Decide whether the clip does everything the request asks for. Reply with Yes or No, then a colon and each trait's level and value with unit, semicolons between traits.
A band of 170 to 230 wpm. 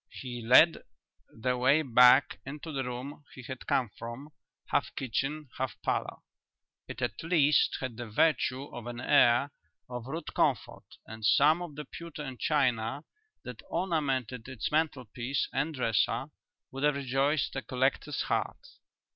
No: average, 145 wpm